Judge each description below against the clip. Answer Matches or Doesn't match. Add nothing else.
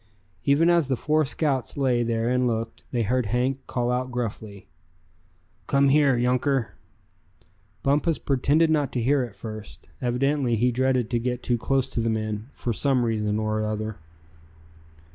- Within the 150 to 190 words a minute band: Matches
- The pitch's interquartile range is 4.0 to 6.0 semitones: Doesn't match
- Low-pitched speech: Matches